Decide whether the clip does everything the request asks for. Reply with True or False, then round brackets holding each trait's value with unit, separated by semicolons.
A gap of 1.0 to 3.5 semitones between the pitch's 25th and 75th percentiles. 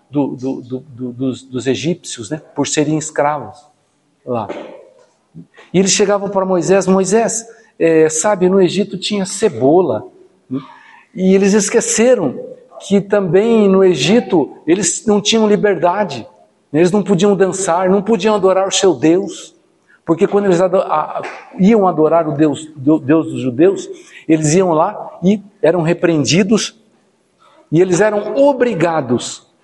False (5.2 semitones)